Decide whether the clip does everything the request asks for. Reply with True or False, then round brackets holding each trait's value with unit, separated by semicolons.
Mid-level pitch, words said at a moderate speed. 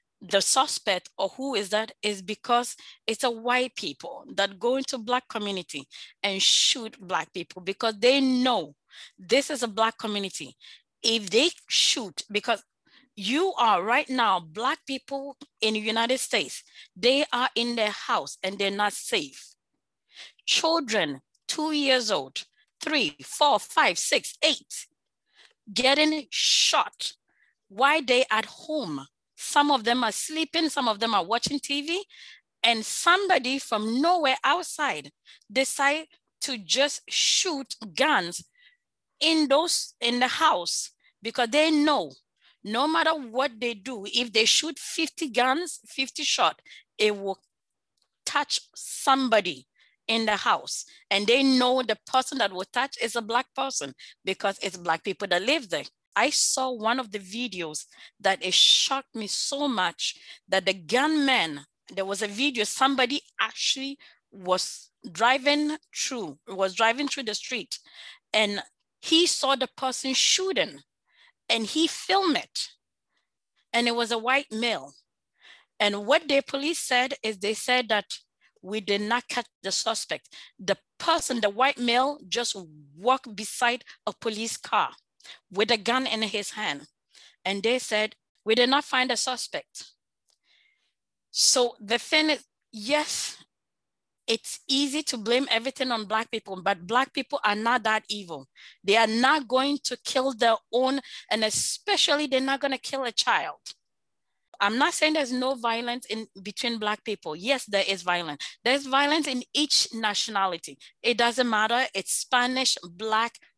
False (240 Hz; 150 wpm)